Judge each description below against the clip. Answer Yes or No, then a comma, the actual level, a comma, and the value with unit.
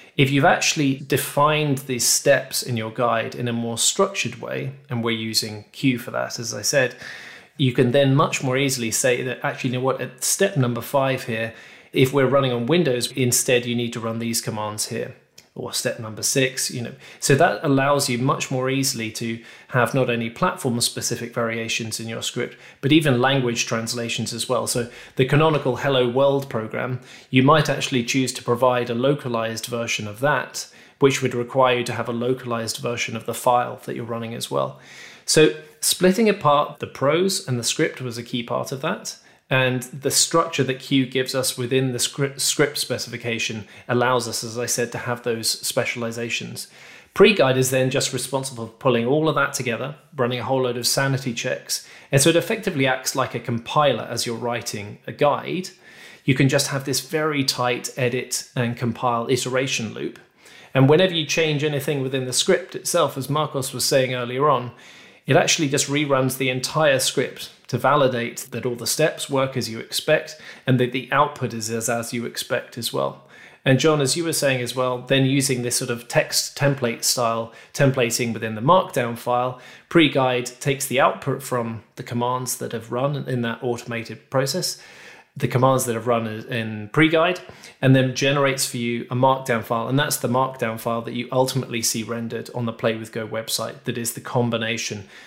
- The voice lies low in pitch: Yes, low, 125 Hz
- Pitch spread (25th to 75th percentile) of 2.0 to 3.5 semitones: Yes, narrow, 2.5 semitones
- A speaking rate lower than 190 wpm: No, average, 195 wpm